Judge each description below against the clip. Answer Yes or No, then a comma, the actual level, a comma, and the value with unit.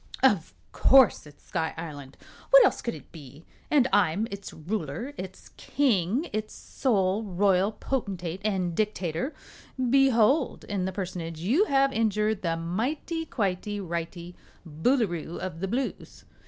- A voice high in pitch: Yes, high, 195 Hz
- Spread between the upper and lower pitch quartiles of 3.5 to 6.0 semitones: Yes, wide, 5.6 semitones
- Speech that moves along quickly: No, slow, 135 wpm